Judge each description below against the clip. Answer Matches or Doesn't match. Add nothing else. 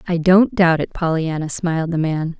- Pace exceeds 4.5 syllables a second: Matches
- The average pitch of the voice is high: Doesn't match